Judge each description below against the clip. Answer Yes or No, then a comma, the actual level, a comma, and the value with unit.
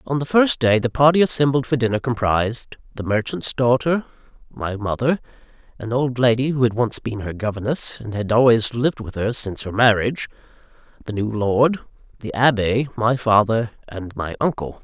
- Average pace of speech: Yes, average, 175 wpm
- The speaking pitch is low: Yes, low, 120 Hz